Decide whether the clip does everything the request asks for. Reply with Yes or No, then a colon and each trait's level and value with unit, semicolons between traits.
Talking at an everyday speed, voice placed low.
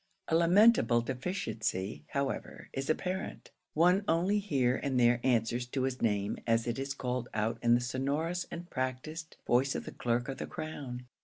Yes: average, 170 wpm; low, 130 Hz